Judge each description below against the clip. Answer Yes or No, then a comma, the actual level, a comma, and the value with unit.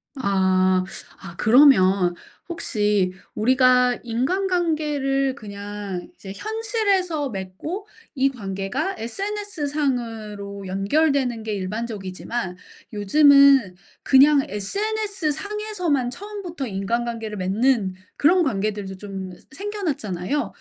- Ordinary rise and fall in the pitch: No, wide, 7.3 semitones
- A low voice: No, high, 245 Hz